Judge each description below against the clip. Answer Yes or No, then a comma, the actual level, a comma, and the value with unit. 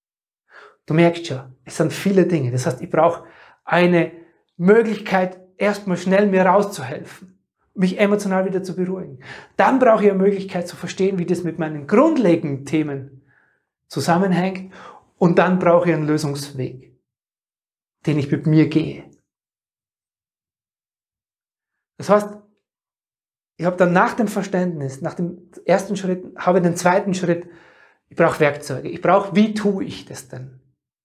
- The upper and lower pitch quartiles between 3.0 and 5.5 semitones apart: Yes, average, 3.4 semitones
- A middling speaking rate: Yes, average, 140 wpm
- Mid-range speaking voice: Yes, medium, 175 Hz